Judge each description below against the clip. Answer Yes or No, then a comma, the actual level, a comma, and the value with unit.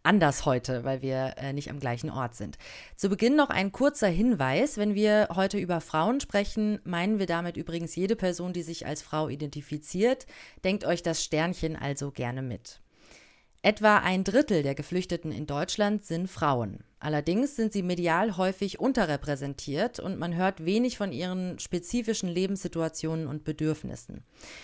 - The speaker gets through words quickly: No, average, 160 wpm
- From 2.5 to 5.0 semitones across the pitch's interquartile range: No, wide, 5.4 semitones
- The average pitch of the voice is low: No, medium, 175 Hz